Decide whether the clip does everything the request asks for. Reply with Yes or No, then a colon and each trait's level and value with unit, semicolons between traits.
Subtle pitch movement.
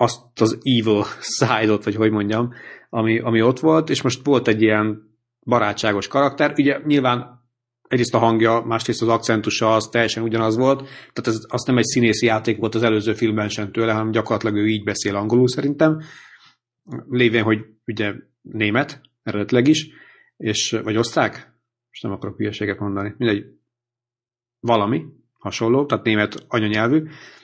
Yes: narrow, 2.1 semitones